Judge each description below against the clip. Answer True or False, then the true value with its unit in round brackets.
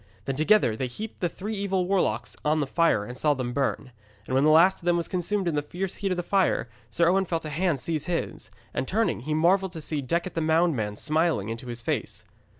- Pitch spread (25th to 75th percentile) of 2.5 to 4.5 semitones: False (5.3 semitones)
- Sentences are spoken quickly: True (240 wpm)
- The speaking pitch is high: False (160 Hz)